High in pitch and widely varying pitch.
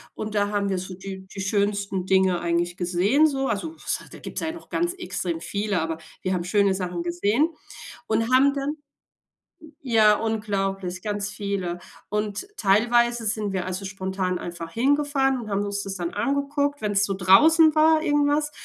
Yes: high, 205 Hz; wide, 6.0 semitones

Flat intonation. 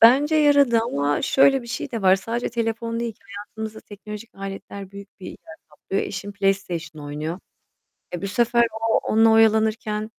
No: average, 3.0 semitones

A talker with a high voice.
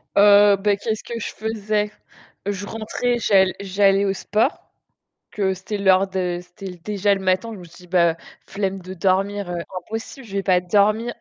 Yes: high, 200 Hz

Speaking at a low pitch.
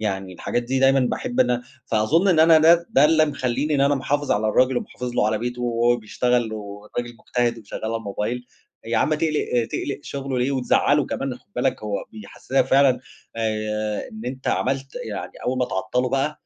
Yes: low, 125 Hz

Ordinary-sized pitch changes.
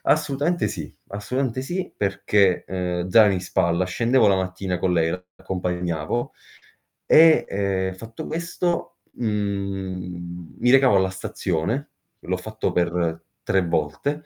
Yes: average, 4.4 semitones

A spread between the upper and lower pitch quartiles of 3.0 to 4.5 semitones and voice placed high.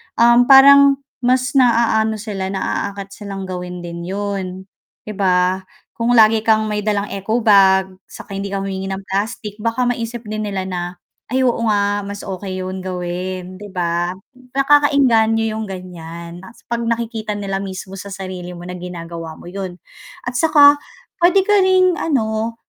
Yes: average, 3.7 semitones; high, 200 Hz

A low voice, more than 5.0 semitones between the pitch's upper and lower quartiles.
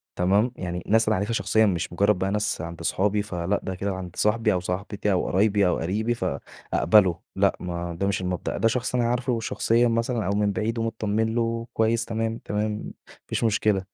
No: low, 105 Hz; average, 3.3 semitones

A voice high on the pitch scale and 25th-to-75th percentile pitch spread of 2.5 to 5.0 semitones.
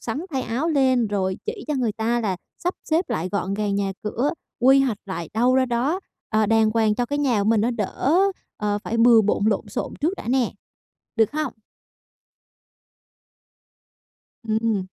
Yes: high, 230 Hz; average, 3.9 semitones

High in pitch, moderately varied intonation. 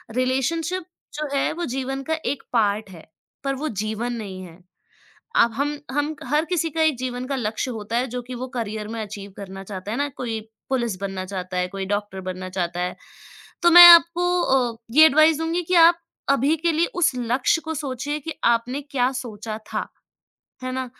No: very high, 250 Hz; wide, 6.2 semitones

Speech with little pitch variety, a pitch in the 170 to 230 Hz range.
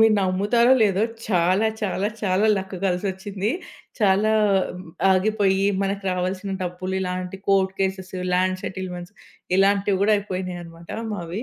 Yes: narrow, 1.6 semitones; high, 190 Hz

